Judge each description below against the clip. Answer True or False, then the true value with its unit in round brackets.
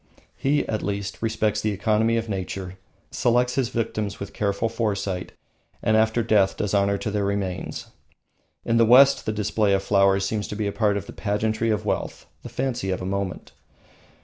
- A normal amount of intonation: False (2.1 semitones)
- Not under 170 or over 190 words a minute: True (185 wpm)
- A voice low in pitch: True (105 Hz)